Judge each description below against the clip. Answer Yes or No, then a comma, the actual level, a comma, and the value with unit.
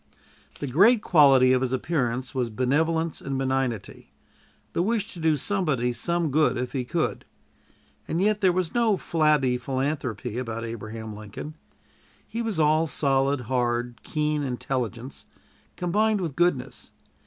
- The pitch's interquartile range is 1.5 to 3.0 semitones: No, average, 5.1 semitones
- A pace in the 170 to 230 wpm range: No, average, 140 wpm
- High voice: No, medium, 140 Hz